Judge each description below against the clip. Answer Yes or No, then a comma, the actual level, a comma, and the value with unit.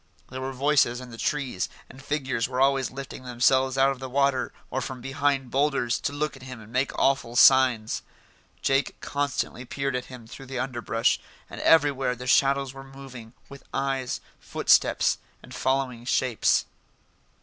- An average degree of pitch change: No, narrow, 1.5 semitones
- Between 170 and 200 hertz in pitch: No, low, 130 Hz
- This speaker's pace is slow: No, average, 165 wpm